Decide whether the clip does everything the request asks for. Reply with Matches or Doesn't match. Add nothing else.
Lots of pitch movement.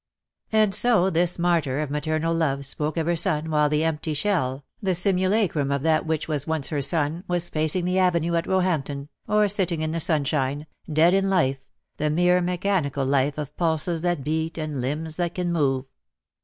Doesn't match